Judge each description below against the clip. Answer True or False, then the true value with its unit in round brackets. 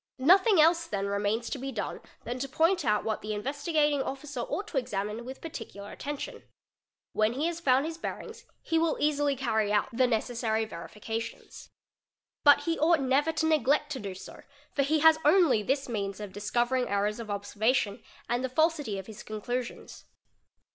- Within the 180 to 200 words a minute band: True (185 wpm)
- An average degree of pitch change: False (5.8 semitones)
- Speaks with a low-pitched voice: False (255 Hz)